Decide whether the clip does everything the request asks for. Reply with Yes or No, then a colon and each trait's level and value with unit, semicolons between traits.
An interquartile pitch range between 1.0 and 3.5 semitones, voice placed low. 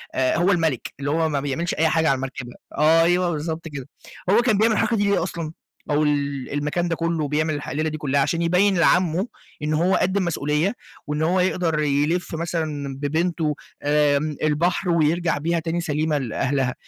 No: average, 2.8 semitones; medium, 160 Hz